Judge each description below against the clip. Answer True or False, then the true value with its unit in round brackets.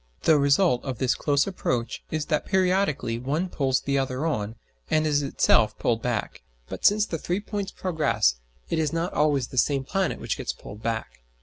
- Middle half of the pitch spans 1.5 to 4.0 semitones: False (5.1 semitones)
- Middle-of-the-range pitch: True (145 Hz)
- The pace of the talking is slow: False (190 wpm)